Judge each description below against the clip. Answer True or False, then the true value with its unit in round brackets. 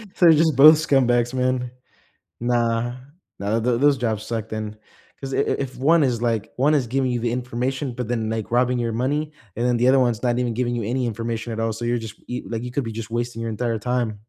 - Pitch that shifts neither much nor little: False (1.9 semitones)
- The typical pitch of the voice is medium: False (120 Hz)